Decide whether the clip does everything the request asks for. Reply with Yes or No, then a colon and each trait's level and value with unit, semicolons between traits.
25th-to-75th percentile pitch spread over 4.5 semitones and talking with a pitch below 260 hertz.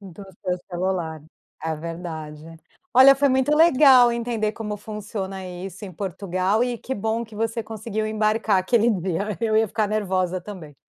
No: average, 3.6 semitones; high, 210 Hz